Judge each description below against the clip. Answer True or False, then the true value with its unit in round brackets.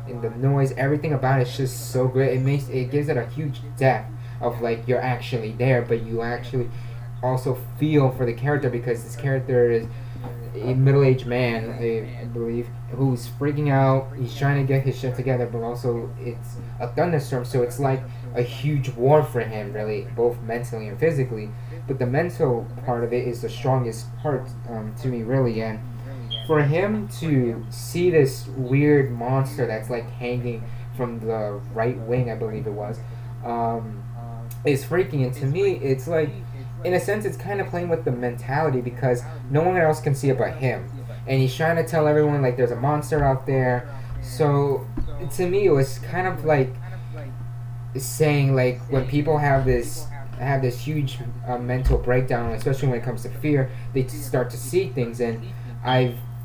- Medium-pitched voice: False (125 Hz)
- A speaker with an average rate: True (185 wpm)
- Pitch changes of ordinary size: False (1.9 semitones)